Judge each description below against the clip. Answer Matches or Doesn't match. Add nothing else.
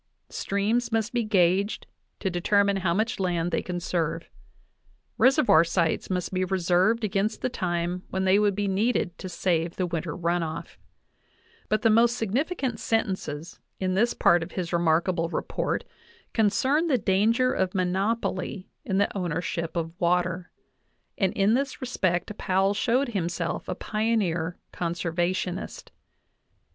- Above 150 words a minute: Doesn't match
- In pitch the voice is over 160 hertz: Matches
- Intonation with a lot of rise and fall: Doesn't match